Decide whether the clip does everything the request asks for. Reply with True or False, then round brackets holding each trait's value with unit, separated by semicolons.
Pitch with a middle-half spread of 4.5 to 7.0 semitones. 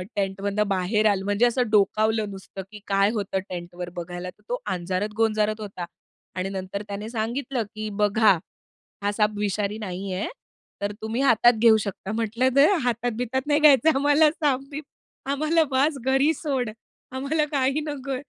True (4.9 semitones)